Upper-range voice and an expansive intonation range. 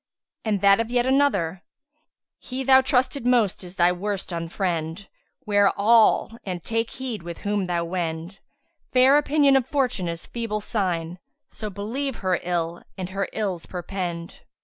Yes: high, 200 Hz; wide, 5.8 semitones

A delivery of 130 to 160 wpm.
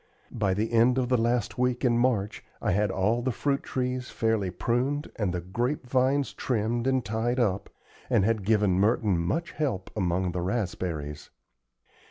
No: average, 170 wpm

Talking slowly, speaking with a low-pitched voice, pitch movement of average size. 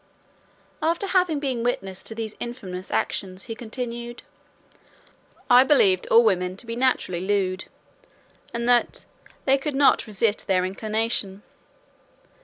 No: slow, 125 wpm; high, 230 Hz; average, 4.5 semitones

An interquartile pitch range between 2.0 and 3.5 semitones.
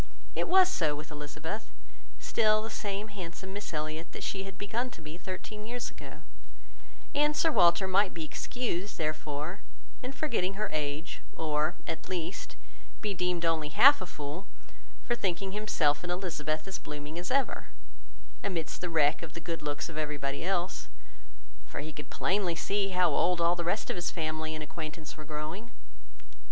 No: average, 4.5 semitones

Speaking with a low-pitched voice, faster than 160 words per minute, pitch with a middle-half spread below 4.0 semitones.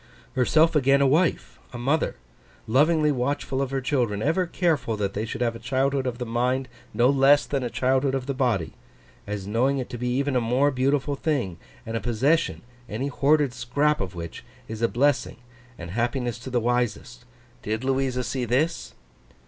Yes: low, 130 Hz; average, 180 wpm; average, 2.9 semitones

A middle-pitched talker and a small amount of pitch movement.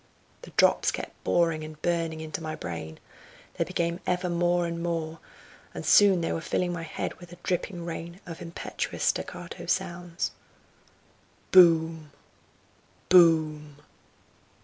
Yes: medium, 170 Hz; narrow, 1.6 semitones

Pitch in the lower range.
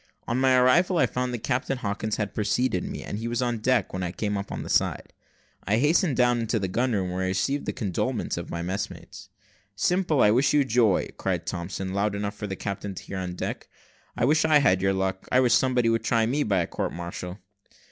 Yes: low, 110 Hz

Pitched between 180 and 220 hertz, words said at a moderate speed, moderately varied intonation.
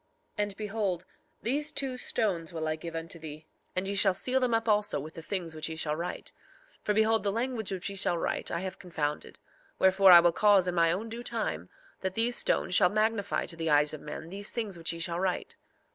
No: high, 190 Hz; fast, 235 wpm; average, 4.4 semitones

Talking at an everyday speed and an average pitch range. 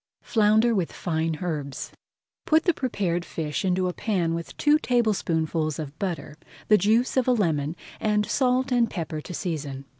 No: average, 160 wpm; wide, 6.1 semitones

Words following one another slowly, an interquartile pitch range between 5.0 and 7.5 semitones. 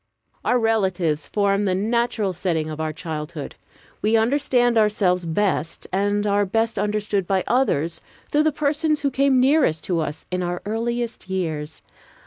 No: average, 150 wpm; wide, 5.5 semitones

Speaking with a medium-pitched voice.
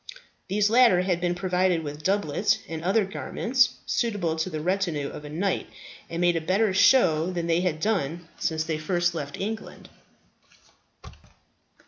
Yes: medium, 175 Hz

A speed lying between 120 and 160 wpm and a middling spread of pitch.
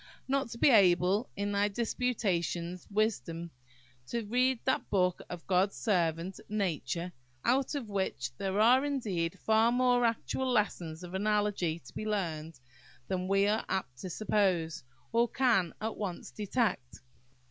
Yes: average, 145 wpm; average, 4.7 semitones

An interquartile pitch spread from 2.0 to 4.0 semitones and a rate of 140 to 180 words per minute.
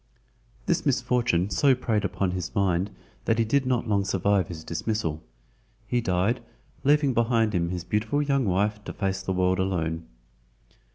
No: average, 4.4 semitones; average, 155 wpm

